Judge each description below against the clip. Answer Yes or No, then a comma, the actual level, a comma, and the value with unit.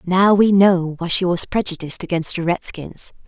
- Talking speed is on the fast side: No, average, 185 wpm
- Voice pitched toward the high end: No, medium, 180 Hz